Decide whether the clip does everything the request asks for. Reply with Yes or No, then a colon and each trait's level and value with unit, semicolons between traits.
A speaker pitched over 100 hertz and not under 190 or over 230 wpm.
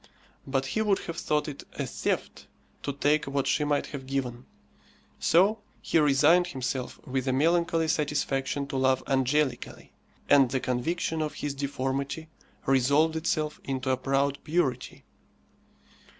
No: medium, 140 Hz; average, 140 wpm